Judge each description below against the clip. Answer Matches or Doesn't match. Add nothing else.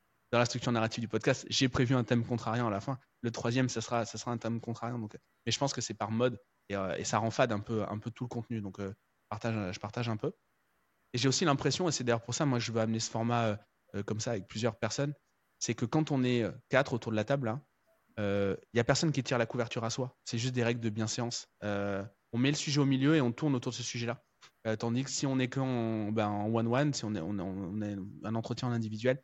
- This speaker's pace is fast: Matches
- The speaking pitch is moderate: Doesn't match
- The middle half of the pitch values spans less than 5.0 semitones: Matches